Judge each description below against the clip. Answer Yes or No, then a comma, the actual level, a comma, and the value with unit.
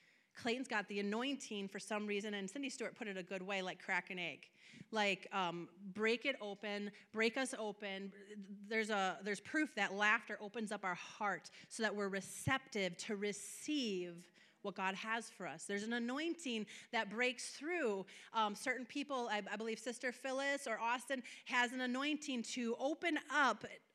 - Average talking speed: Yes, average, 175 wpm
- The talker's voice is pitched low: No, high, 215 Hz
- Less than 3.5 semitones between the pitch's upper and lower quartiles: No, average, 4.0 semitones